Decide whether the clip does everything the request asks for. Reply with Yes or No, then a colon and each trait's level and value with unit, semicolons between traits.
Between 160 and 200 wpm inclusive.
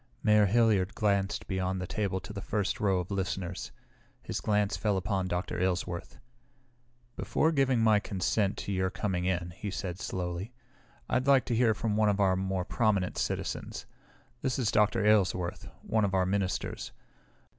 Yes: average, 165 wpm